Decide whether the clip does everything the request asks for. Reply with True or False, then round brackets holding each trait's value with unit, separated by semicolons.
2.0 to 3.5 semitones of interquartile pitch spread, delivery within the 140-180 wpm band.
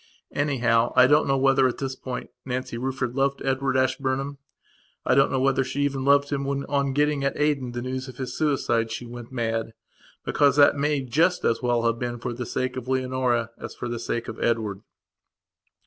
False (2.4 semitones; 200 wpm)